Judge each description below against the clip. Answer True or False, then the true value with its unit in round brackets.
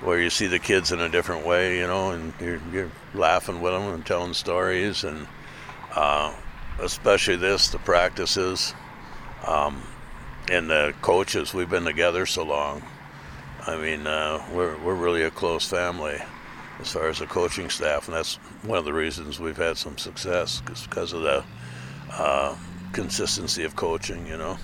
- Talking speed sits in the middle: True (170 wpm)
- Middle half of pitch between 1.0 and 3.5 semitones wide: True (2.5 semitones)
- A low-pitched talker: True (85 Hz)